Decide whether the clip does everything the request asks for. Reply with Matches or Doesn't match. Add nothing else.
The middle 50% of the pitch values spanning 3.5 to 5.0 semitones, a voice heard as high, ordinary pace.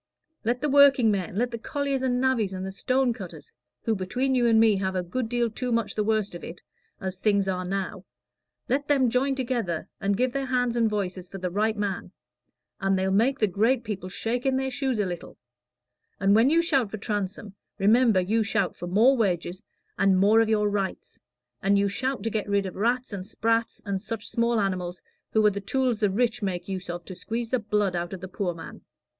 Doesn't match